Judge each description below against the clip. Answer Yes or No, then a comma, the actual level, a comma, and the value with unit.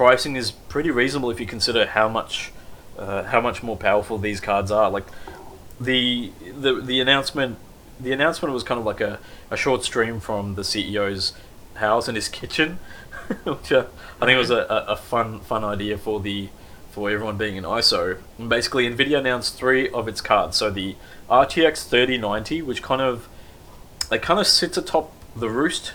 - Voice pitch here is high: No, low, 110 Hz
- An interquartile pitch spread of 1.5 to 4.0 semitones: Yes, average, 3.6 semitones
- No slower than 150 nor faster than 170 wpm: No, average, 185 wpm